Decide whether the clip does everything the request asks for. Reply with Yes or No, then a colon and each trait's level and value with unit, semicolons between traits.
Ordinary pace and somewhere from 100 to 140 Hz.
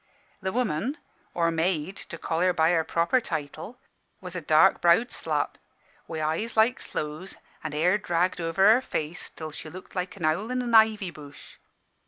No: average, 180 wpm; medium, 175 Hz